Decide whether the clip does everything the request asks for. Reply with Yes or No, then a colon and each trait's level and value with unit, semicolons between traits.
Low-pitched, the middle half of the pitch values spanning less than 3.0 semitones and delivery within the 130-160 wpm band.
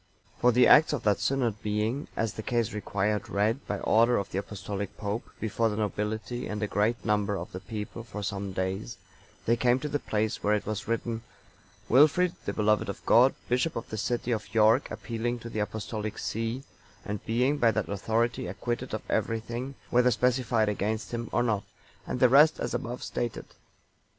No: low, 110 Hz; narrow, 2.6 semitones; average, 190 wpm